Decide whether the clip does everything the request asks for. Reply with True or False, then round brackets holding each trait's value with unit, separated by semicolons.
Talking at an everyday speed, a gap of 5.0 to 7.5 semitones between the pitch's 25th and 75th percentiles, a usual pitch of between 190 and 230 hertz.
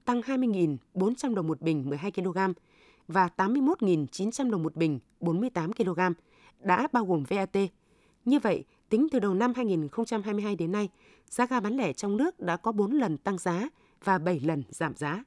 True (175 wpm; 5.3 semitones; 195 Hz)